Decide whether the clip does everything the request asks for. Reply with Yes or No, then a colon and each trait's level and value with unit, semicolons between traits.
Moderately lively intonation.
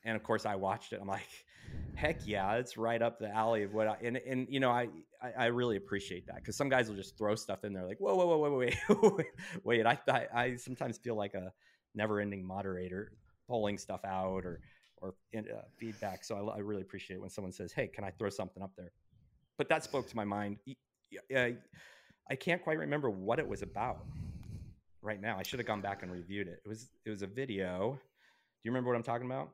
Yes: average, 3.9 semitones